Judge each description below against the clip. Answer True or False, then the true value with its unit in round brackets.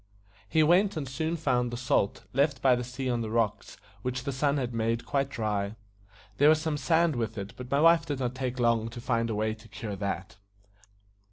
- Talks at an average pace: False (215 wpm)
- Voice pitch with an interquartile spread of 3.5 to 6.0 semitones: True (3.8 semitones)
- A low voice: True (125 Hz)